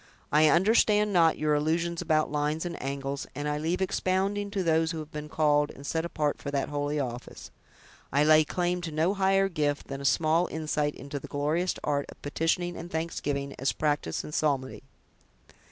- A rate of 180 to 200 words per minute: Yes, average, 185 wpm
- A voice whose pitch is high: No, medium, 155 Hz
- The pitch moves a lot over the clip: No, average, 2.9 semitones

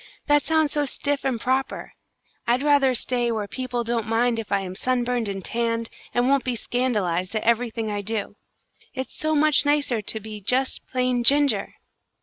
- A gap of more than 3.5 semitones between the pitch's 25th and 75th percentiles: No, average, 3.2 semitones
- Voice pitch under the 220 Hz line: No, high, 245 Hz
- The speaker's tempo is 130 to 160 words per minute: No, average, 175 wpm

